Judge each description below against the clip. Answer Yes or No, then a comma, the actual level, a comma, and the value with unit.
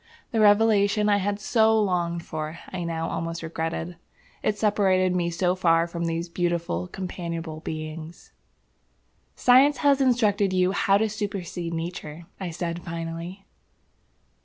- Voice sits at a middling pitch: Yes, medium, 175 Hz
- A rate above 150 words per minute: No, slow, 135 wpm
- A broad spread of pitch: No, average, 3.5 semitones